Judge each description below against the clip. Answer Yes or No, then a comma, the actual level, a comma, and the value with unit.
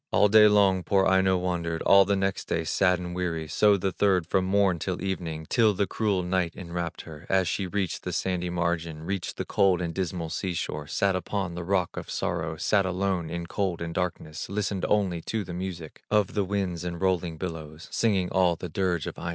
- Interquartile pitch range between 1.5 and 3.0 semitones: Yes, narrow, 2.4 semitones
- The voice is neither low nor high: No, very low, 90 Hz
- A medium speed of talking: No, fast, 210 wpm